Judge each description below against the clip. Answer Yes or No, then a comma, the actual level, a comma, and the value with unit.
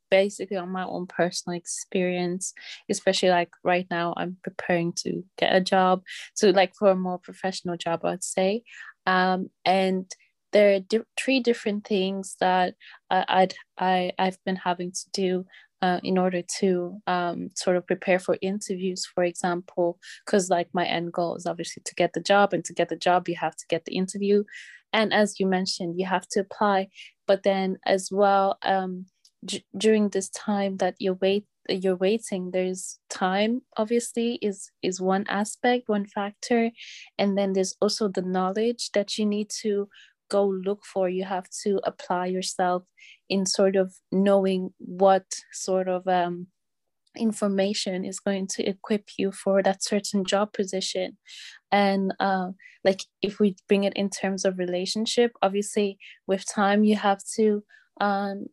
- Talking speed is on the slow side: No, average, 165 wpm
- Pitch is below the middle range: No, high, 190 Hz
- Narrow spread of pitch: Yes, narrow, 1.6 semitones